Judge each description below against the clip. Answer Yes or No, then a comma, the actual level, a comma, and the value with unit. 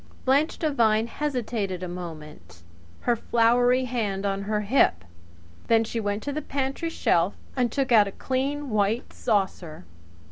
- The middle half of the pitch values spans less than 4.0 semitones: No, average, 4.7 semitones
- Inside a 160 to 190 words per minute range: No, average, 145 wpm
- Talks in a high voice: Yes, high, 225 Hz